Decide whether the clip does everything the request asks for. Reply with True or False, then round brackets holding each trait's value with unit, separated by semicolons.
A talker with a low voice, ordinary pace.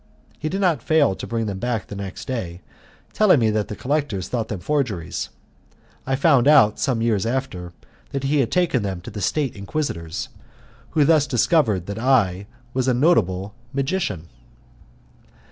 True (120 Hz; 165 wpm)